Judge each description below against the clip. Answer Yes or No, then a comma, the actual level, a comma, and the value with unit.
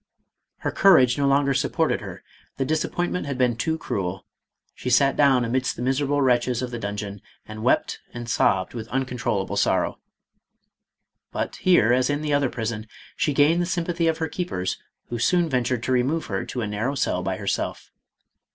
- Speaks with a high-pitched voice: No, low, 130 Hz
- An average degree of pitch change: Yes, average, 3.9 semitones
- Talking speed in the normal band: Yes, average, 180 wpm